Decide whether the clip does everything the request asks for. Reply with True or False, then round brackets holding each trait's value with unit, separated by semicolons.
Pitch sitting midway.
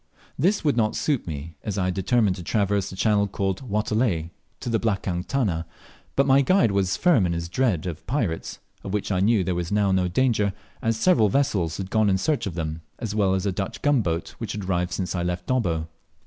False (100 Hz)